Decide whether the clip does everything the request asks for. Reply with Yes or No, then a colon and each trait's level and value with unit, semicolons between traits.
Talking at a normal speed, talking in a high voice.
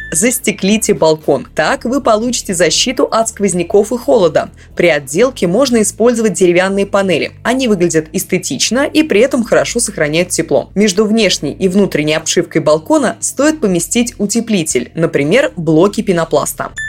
Yes: average, 130 wpm; high, 205 Hz